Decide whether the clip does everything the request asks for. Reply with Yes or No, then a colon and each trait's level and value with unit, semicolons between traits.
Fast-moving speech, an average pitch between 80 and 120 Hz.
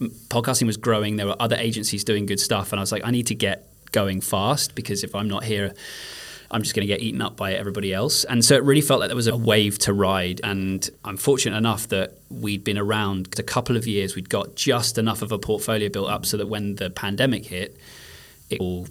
Yes: fast, 240 wpm; low, 105 Hz